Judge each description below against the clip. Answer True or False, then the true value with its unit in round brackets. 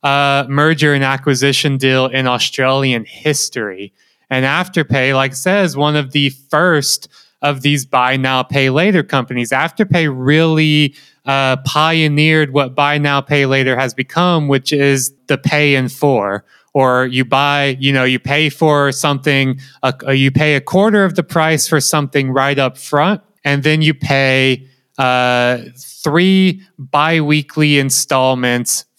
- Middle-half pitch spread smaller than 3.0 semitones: True (2.4 semitones)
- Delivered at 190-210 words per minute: False (145 wpm)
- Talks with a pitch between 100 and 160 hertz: True (140 Hz)